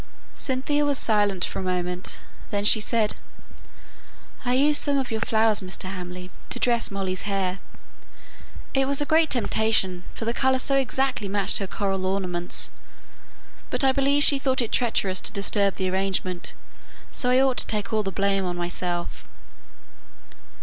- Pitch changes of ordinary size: No, wide, 5.7 semitones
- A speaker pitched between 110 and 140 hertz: No, high, 210 Hz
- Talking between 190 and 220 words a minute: No, average, 165 wpm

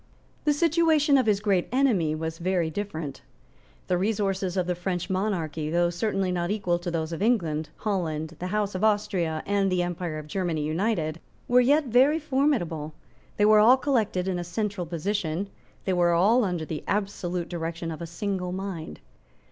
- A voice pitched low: No, medium, 185 Hz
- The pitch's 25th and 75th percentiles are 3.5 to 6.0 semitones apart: Yes, average, 3.9 semitones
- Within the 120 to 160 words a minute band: No, average, 175 wpm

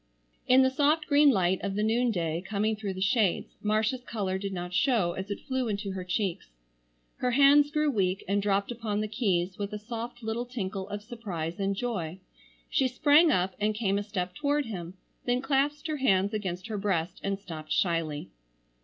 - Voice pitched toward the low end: No, high, 210 Hz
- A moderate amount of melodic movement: Yes, average, 4.6 semitones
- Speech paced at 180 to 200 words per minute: Yes, average, 190 wpm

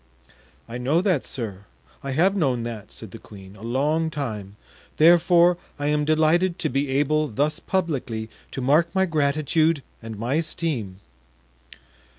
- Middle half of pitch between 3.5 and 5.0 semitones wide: No, wide, 5.5 semitones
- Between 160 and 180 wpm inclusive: No, average, 150 wpm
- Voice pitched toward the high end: No, medium, 145 Hz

